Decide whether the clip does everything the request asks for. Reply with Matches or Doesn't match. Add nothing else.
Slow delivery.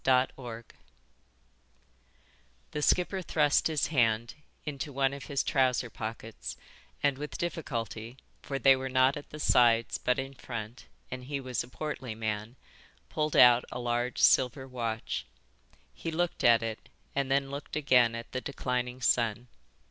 Doesn't match